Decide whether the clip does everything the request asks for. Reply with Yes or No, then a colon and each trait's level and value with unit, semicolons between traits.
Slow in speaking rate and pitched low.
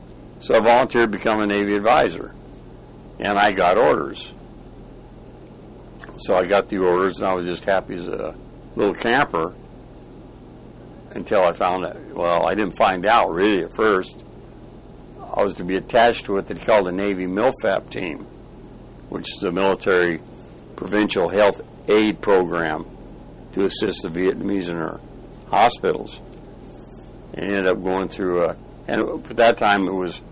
No: average, 155 wpm; very low, 95 Hz